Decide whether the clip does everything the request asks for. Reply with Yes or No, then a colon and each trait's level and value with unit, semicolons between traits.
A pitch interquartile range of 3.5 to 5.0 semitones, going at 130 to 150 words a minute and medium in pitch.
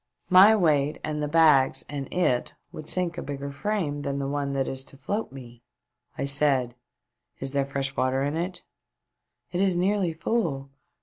No: average, 4.2 semitones; average, 185 wpm; medium, 145 Hz